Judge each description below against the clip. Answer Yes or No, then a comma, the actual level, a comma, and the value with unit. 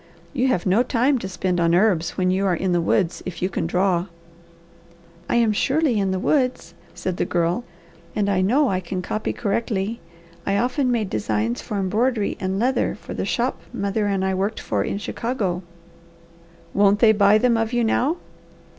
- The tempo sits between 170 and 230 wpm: Yes, average, 190 wpm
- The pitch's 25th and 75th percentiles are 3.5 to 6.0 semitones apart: Yes, average, 4.1 semitones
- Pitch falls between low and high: No, high, 200 Hz